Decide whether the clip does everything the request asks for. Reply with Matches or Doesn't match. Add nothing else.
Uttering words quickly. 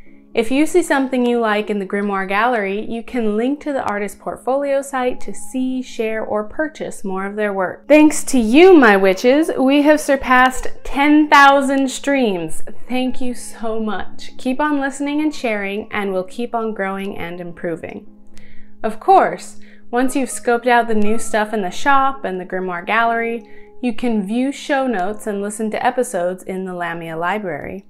Doesn't match